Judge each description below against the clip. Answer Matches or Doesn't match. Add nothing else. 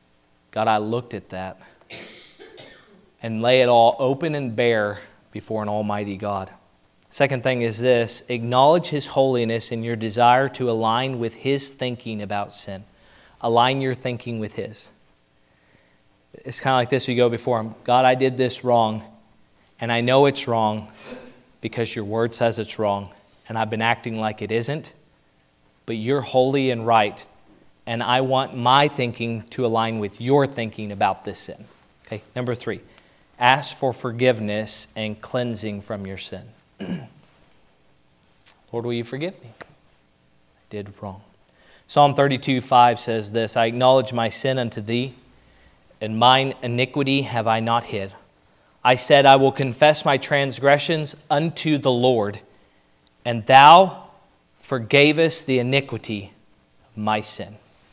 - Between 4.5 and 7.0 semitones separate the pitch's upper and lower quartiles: Doesn't match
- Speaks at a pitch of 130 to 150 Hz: Doesn't match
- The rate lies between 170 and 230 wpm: Doesn't match